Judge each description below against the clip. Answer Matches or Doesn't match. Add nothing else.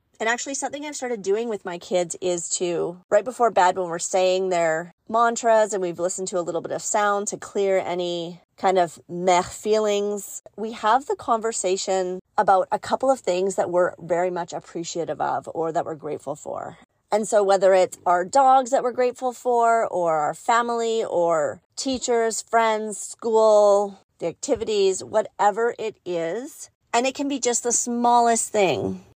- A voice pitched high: Matches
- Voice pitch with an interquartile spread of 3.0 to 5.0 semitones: Matches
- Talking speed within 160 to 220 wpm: Matches